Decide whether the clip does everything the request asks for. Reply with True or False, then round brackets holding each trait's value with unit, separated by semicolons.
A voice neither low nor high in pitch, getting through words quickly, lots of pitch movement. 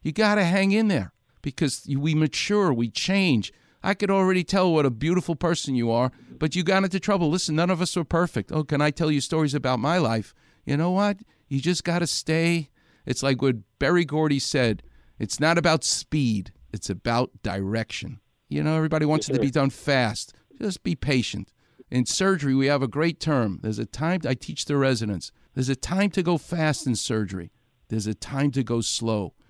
True (145 Hz; 210 wpm; 6.1 semitones)